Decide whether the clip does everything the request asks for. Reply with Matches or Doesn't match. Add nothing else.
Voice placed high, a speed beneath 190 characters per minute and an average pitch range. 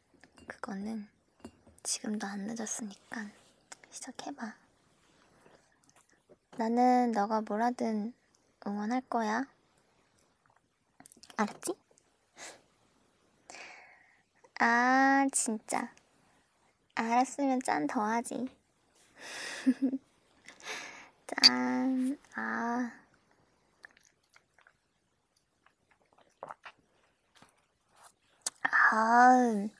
Matches